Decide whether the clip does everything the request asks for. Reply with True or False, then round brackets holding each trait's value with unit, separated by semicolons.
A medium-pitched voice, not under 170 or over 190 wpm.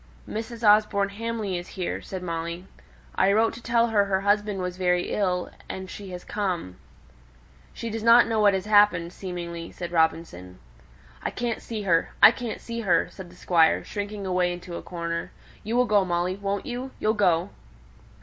False (195 Hz; 180 wpm)